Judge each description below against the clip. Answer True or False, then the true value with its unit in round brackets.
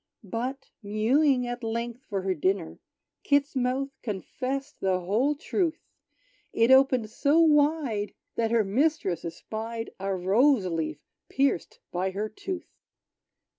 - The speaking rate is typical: False (125 wpm)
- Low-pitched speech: False (235 Hz)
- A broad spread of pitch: True (5.8 semitones)